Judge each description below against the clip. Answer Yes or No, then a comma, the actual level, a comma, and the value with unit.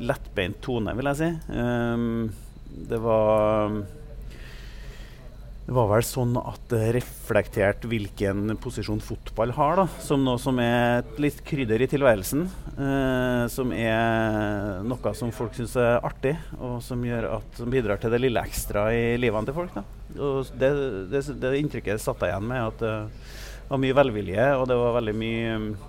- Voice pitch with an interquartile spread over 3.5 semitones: No, average, 3.2 semitones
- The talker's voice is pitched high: No, low, 120 Hz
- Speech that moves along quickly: No, average, 170 wpm